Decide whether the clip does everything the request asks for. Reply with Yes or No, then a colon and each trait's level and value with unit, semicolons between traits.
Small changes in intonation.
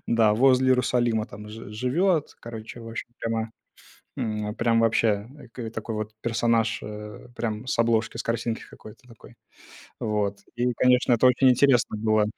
Yes: narrow, 2.2 semitones